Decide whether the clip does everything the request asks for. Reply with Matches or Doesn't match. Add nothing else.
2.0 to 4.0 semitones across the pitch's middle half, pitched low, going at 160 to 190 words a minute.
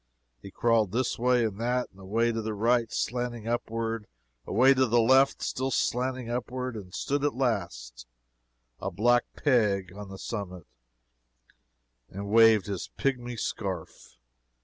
Doesn't match